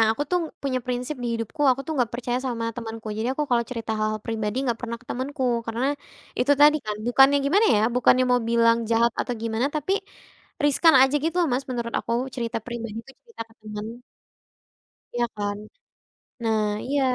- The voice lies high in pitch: Yes, high, 240 Hz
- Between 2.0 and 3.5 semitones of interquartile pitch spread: Yes, average, 2.9 semitones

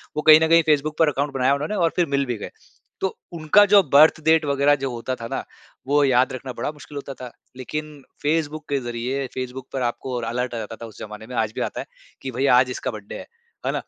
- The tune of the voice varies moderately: Yes, average, 3.4 semitones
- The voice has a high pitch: No, low, 135 Hz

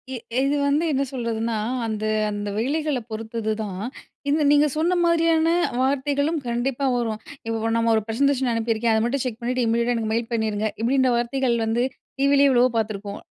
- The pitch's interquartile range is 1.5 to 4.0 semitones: Yes, average, 3.7 semitones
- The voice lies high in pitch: Yes, high, 240 Hz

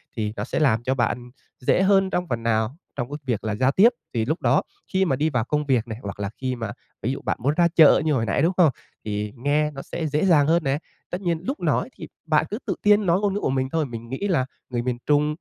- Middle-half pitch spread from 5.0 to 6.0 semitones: Yes, wide, 5.6 semitones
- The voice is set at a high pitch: No, low, 135 Hz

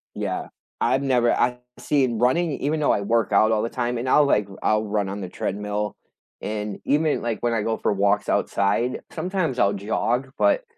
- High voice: No, low, 115 Hz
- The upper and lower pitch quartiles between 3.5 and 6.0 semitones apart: Yes, average, 4.3 semitones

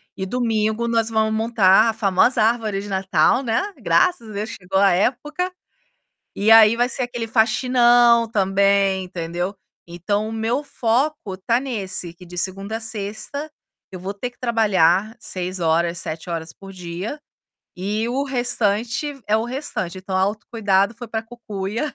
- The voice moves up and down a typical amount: Yes, average, 3.7 semitones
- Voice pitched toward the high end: Yes, high, 215 Hz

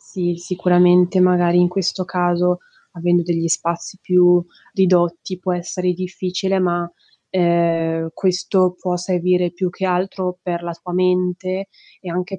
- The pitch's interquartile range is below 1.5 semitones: Yes, narrow, 0.9 semitones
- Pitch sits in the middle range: Yes, medium, 180 Hz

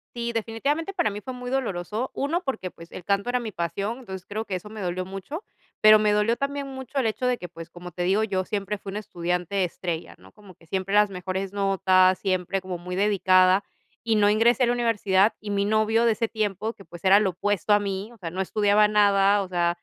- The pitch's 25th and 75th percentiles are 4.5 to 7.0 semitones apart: No, average, 3.1 semitones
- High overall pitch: Yes, high, 205 Hz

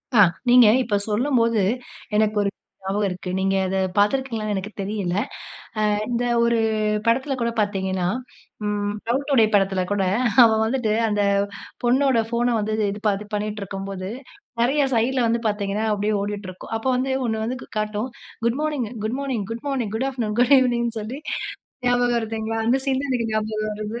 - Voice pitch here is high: Yes, high, 220 Hz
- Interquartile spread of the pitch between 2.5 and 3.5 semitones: Yes, average, 2.9 semitones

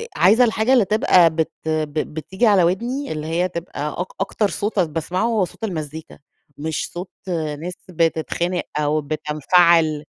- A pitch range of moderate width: Yes, average, 3.8 semitones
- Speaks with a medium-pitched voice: Yes, medium, 170 Hz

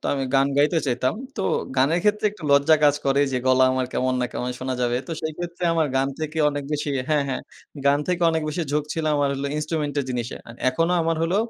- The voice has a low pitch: No, medium, 145 Hz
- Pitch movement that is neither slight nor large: Yes, average, 3.7 semitones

